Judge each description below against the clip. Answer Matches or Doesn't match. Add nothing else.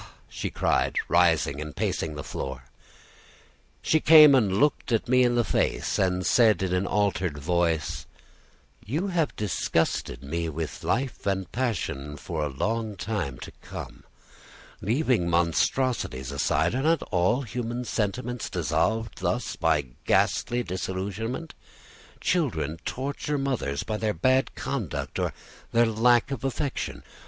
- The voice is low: Matches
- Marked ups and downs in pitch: Matches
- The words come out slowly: Matches